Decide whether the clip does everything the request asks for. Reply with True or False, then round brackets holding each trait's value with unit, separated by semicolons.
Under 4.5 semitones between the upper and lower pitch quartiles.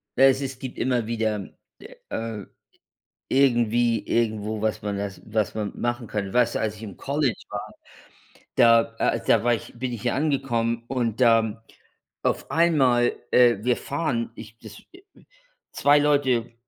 True (2.9 semitones)